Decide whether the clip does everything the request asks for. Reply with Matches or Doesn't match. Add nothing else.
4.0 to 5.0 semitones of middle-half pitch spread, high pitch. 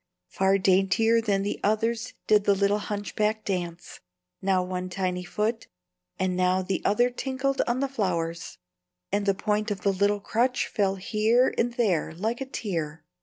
Doesn't match